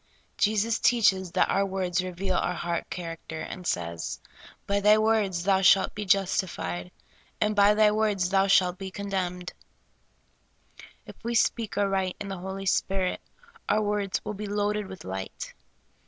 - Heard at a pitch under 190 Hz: No, high, 195 Hz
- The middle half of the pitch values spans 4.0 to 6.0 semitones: No, narrow, 2.4 semitones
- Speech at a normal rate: Yes, average, 155 wpm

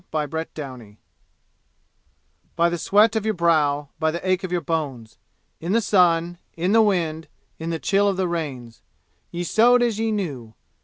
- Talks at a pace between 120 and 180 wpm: Yes, average, 170 wpm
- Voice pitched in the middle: Yes, medium, 170 Hz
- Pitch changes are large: No, average, 4.4 semitones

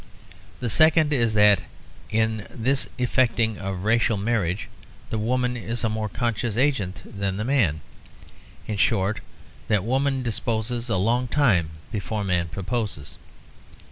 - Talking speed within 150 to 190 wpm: No, slow, 135 wpm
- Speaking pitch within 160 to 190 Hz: No, low, 110 Hz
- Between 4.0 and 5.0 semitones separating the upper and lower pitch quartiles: No, average, 3.5 semitones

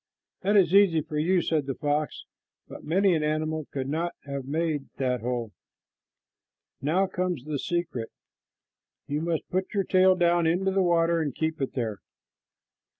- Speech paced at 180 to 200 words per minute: No, average, 160 wpm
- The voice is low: No, medium, 160 Hz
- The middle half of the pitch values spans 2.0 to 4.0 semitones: Yes, average, 3.7 semitones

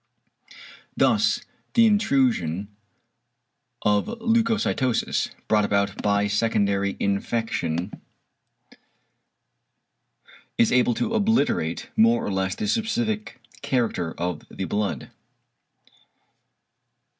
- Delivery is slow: Yes, slow, 85 wpm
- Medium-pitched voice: No, low, 110 Hz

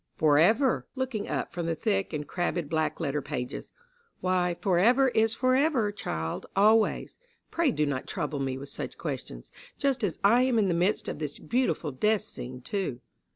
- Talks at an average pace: Yes, average, 180 wpm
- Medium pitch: Yes, medium, 180 Hz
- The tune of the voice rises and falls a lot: Yes, wide, 7.3 semitones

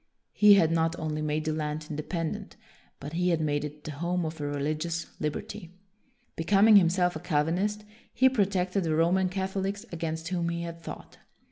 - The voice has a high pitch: No, medium, 165 Hz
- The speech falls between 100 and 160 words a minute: No, average, 180 wpm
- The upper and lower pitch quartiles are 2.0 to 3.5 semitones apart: Yes, average, 3.1 semitones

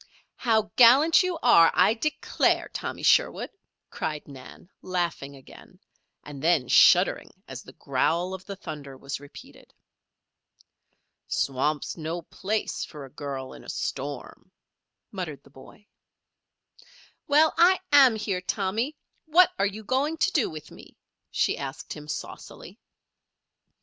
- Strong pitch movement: Yes, wide, 8.3 semitones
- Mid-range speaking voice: Yes, medium, 180 Hz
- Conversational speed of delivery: No, slow, 130 wpm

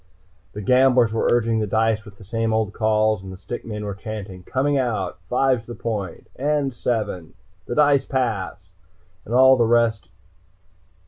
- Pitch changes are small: No, average, 3.2 semitones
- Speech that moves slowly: No, average, 170 wpm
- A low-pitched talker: Yes, low, 115 Hz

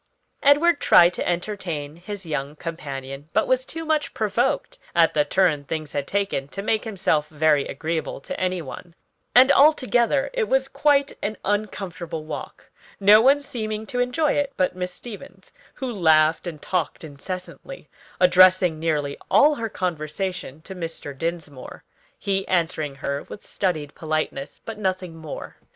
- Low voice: No, medium, 180 Hz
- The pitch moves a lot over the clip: Yes, wide, 5.7 semitones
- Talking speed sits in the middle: Yes, average, 150 wpm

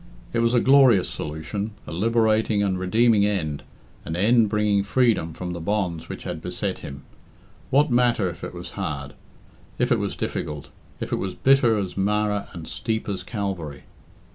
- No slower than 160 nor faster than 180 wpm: Yes, average, 170 wpm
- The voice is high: No, low, 100 Hz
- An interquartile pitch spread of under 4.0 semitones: No, average, 4.5 semitones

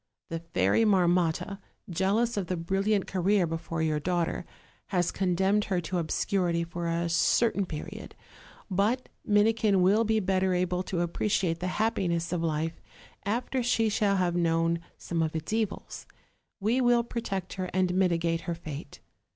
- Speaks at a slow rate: No, average, 150 wpm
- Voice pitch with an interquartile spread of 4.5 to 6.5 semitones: No, average, 3.4 semitones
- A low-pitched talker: No, medium, 180 Hz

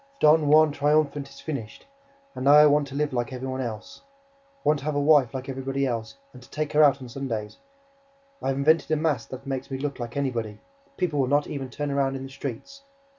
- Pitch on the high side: No, medium, 140 Hz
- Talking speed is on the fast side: Yes, fast, 230 wpm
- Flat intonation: Yes, narrow, 2.2 semitones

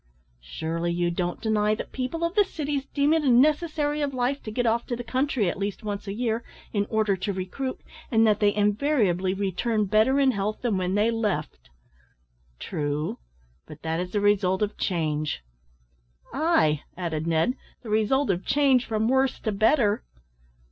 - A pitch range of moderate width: No, wide, 5.7 semitones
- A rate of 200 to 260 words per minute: No, average, 175 wpm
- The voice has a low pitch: No, high, 215 Hz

